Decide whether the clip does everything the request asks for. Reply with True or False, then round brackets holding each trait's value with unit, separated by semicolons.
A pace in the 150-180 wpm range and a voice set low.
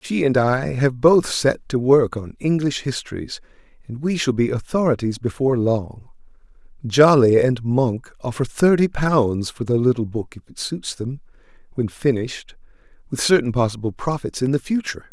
True (165 wpm; 130 Hz)